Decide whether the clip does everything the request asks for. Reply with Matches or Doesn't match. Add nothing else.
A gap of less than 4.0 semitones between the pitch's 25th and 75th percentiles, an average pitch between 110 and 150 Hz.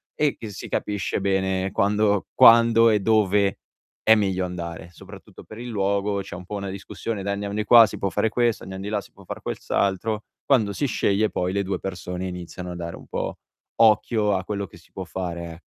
Doesn't match